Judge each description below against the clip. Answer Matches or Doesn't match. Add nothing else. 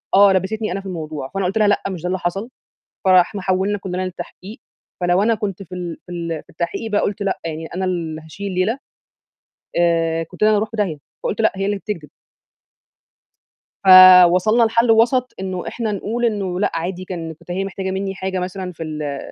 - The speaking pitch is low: Doesn't match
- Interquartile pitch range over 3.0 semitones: Doesn't match